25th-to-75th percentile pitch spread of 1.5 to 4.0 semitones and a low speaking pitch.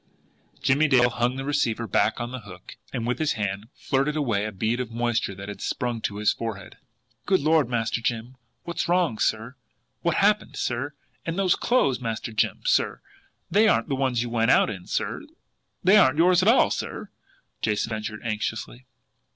No: average, 5.0 semitones; low, 120 Hz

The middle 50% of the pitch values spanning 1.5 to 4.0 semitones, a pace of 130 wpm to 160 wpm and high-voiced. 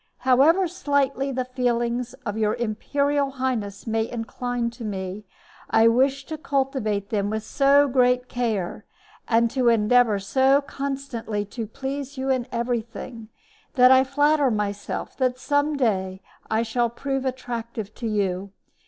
Yes: average, 3.5 semitones; average, 140 wpm; high, 245 Hz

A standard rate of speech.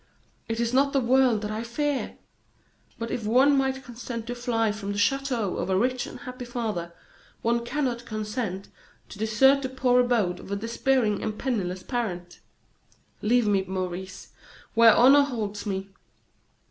Yes: average, 160 wpm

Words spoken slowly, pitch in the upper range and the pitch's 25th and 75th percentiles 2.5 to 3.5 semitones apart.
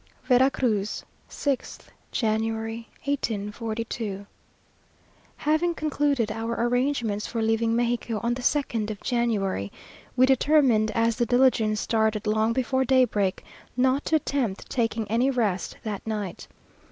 Yes: slow, 120 wpm; high, 230 Hz; average, 3.1 semitones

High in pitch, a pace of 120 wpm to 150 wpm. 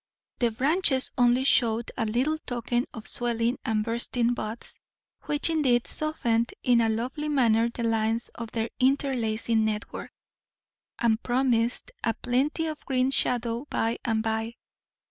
Yes: high, 240 Hz; average, 140 wpm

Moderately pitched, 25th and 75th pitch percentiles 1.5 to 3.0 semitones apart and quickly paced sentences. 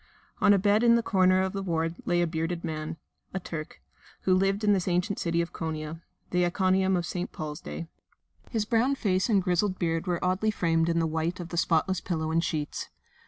Yes: medium, 180 Hz; average, 2.7 semitones; fast, 210 wpm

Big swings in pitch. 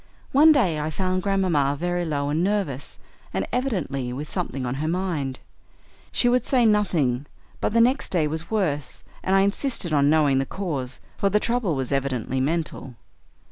Yes: wide, 6.2 semitones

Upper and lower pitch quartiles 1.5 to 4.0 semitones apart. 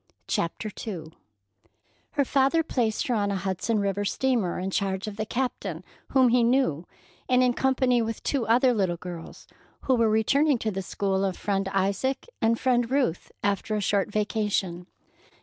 No: average, 4.4 semitones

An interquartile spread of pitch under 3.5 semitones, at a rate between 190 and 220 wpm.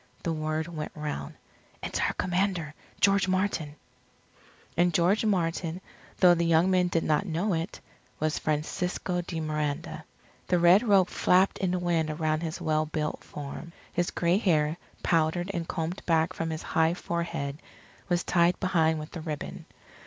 No: narrow, 2.4 semitones; average, 160 wpm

